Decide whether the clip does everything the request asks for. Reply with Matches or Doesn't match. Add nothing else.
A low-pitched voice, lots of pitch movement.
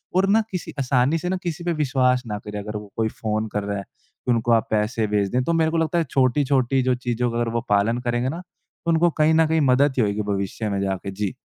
Matches